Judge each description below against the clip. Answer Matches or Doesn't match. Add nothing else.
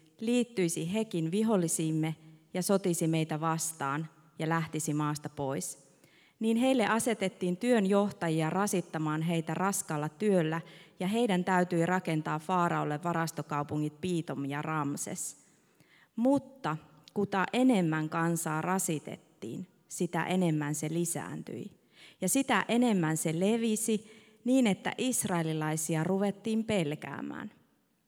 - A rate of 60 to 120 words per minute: Matches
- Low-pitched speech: Doesn't match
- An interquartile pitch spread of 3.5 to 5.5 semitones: Matches